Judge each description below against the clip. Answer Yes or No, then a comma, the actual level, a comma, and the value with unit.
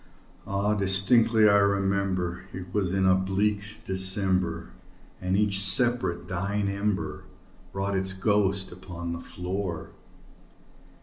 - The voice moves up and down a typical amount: No, narrow, 1.6 semitones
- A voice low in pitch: Yes, very low, 95 Hz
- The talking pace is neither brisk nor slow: No, slow, 115 wpm